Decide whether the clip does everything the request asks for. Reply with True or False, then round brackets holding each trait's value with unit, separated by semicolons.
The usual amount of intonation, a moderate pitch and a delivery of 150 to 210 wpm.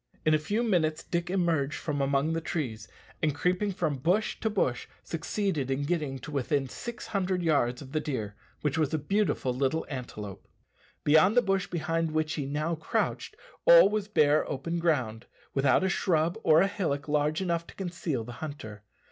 True (4.2 semitones; 155 Hz; 180 wpm)